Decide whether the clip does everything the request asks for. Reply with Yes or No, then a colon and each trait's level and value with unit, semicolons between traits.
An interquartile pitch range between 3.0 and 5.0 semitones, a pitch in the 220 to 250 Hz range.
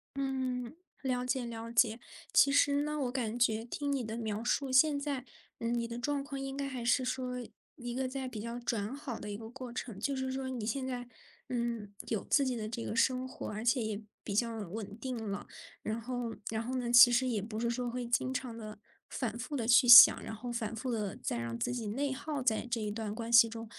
No: narrow, 2.6 semitones; high, 240 Hz